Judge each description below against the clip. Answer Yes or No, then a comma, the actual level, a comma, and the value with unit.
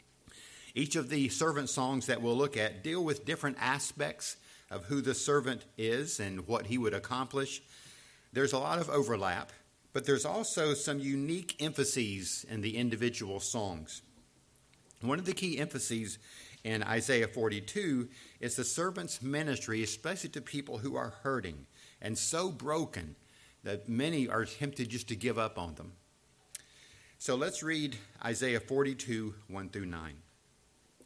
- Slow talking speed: No, average, 150 wpm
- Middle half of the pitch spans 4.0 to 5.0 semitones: Yes, average, 4.7 semitones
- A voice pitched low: Yes, low, 125 Hz